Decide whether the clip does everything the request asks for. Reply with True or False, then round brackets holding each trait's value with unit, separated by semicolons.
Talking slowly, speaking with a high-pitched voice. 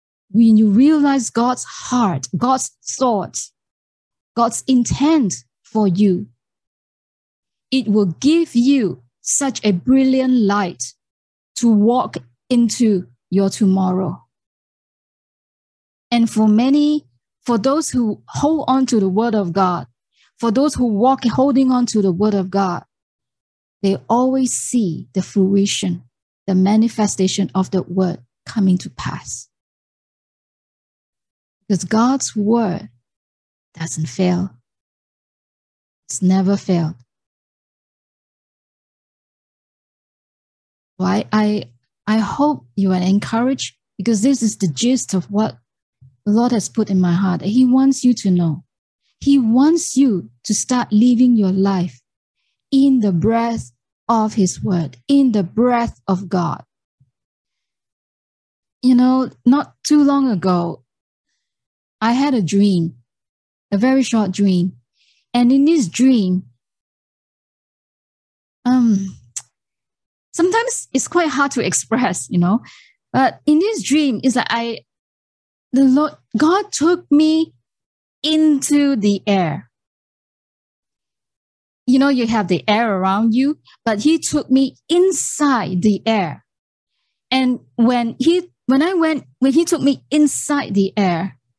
True (120 wpm; 220 Hz)